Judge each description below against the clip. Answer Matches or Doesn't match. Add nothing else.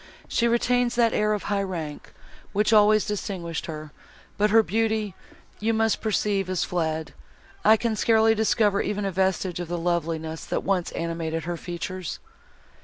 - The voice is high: Matches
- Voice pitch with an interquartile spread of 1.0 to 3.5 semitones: Doesn't match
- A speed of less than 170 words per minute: Matches